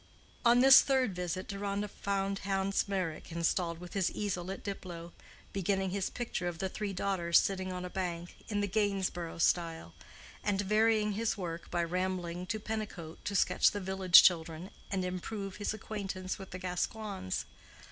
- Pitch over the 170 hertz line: Yes, high, 190 Hz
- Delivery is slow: No, average, 165 wpm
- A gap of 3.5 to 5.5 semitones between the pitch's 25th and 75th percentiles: No, narrow, 2.4 semitones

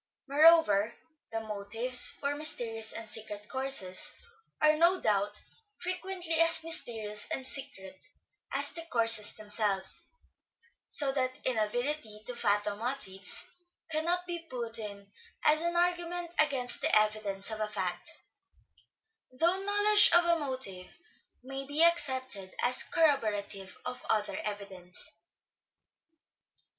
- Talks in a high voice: Yes, very high, 250 Hz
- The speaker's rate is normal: No, slow, 115 wpm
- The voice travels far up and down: Yes, wide, 7.1 semitones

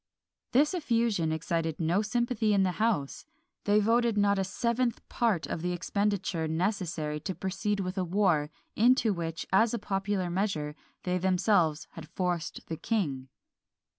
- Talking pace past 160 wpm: No, average, 150 wpm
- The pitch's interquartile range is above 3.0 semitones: Yes, average, 4.3 semitones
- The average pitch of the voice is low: No, high, 190 Hz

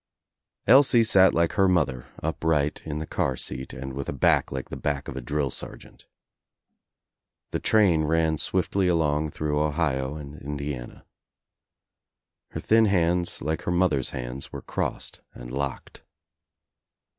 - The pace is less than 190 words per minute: Yes, average, 145 wpm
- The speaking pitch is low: Yes, very low, 75 Hz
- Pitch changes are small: No, average, 4.1 semitones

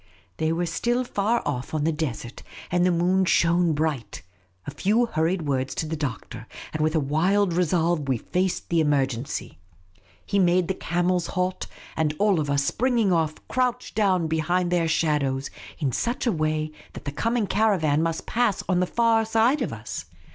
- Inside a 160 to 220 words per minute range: Yes, average, 180 wpm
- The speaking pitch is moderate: Yes, medium, 170 Hz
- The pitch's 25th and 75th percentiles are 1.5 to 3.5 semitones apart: No, average, 4.3 semitones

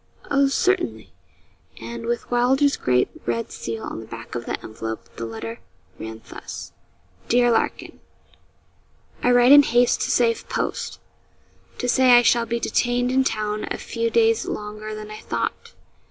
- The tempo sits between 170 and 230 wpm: No, average, 155 wpm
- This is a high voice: Yes, high, 230 Hz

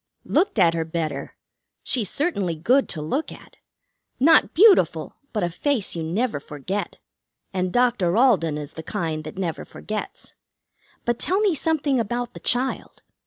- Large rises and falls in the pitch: Yes, wide, 8.0 semitones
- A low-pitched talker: No, high, 205 Hz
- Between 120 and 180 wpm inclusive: Yes, average, 155 wpm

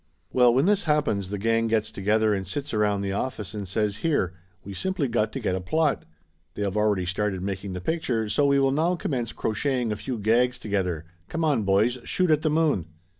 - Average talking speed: No, fast, 220 wpm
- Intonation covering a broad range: Yes, wide, 5.7 semitones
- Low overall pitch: Yes, low, 110 Hz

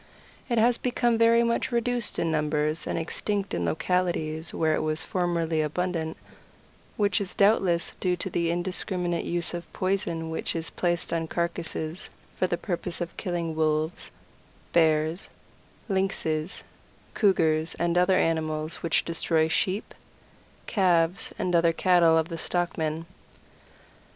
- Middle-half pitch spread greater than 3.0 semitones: No, narrow, 2.4 semitones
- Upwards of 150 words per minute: No, slow, 135 wpm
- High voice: No, medium, 170 Hz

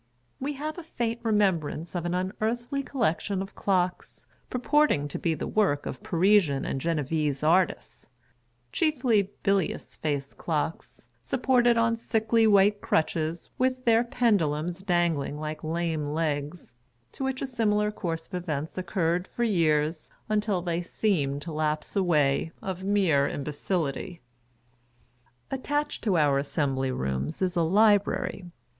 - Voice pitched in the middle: Yes, medium, 175 Hz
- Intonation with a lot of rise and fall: Yes, wide, 6.1 semitones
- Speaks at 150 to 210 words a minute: No, average, 140 wpm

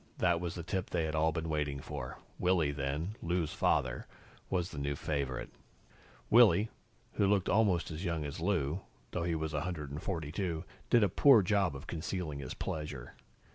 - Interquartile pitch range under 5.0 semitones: Yes, average, 3.6 semitones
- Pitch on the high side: No, very low, 80 Hz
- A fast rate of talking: No, average, 170 wpm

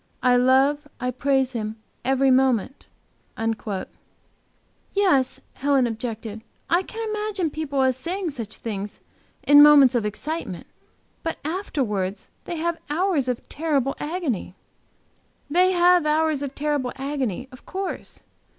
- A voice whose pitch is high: Yes, very high, 275 Hz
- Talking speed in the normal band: No, slow, 125 wpm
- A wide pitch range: No, average, 4.5 semitones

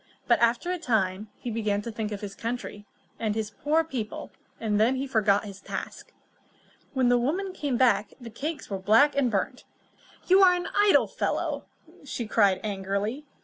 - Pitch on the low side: No, high, 230 Hz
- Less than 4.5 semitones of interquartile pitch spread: No, average, 5.0 semitones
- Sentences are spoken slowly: No, average, 185 wpm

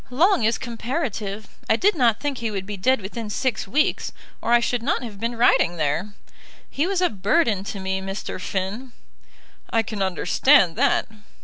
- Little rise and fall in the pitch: No, average, 5.0 semitones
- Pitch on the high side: Yes, high, 225 Hz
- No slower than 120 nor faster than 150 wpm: No, average, 180 wpm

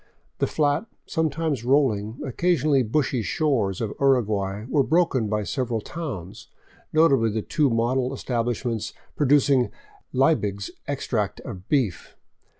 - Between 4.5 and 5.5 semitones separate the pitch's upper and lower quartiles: Yes, average, 5.0 semitones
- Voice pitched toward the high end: No, low, 130 Hz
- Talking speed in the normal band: No, slow, 125 wpm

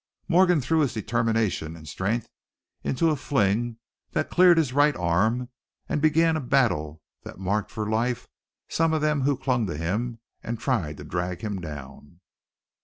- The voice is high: No, low, 115 Hz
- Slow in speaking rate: No, average, 165 wpm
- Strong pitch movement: Yes, wide, 7.9 semitones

